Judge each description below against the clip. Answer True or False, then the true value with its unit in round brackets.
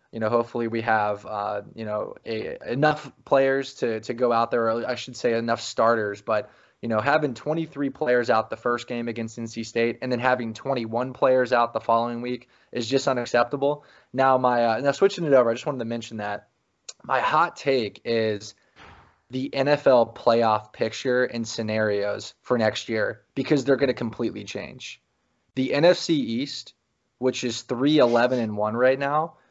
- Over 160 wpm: True (185 wpm)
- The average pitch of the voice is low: True (120 Hz)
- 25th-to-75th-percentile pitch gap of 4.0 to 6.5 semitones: False (2.8 semitones)